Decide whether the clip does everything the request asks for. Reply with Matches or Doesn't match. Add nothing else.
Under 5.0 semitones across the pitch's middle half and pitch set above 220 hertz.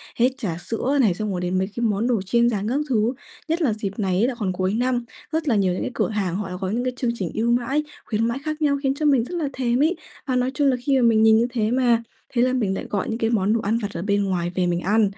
Matches